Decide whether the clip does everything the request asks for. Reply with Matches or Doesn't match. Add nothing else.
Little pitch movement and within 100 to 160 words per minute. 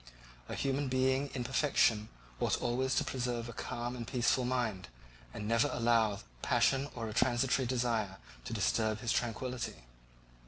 Matches